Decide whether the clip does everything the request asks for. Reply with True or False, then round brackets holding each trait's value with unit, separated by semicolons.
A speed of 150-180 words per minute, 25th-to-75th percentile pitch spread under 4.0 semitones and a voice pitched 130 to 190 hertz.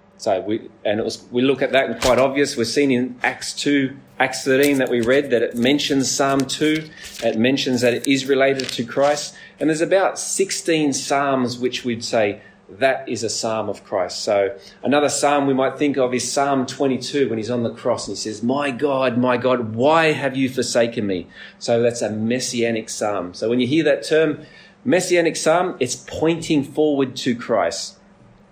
False (200 wpm; 2.8 semitones; 135 Hz)